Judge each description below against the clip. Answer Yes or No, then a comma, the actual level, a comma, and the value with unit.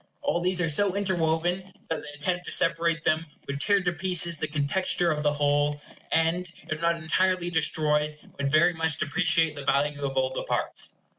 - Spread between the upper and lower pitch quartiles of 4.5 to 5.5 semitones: No, average, 3.1 semitones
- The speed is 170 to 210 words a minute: Yes, average, 190 wpm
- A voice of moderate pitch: Yes, medium, 160 Hz